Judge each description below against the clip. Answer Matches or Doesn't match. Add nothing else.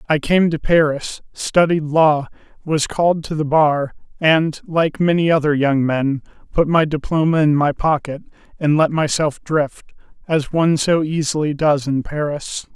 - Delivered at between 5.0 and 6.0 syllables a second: Doesn't match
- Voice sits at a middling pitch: Matches